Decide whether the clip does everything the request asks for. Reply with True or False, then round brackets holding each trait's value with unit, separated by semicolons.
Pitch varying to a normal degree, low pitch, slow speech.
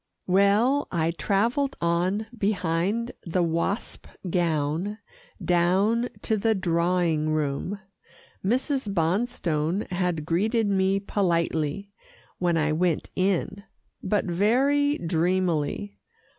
False (3.7 semitones; 185 Hz; 95 wpm)